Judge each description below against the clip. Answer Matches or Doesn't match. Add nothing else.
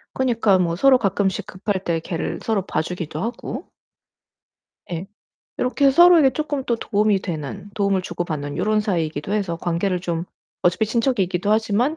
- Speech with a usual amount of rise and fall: Matches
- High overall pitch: Matches